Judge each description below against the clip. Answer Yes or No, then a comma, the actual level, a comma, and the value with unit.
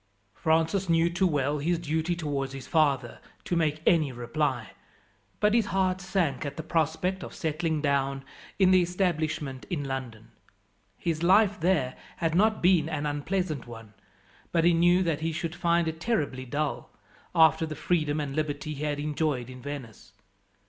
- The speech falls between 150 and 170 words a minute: Yes, average, 165 wpm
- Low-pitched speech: No, medium, 155 Hz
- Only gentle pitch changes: No, average, 3.5 semitones